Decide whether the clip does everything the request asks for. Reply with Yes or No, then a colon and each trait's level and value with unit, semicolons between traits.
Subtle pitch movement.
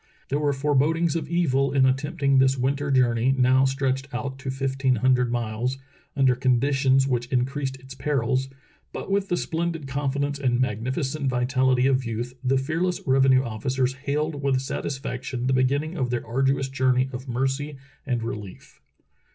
Yes: narrow, 1.7 semitones